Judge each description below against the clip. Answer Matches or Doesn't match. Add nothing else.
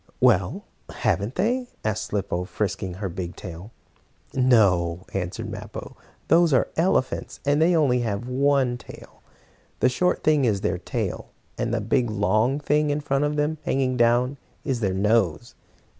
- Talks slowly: Doesn't match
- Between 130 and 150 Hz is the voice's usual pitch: Doesn't match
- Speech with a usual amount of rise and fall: Doesn't match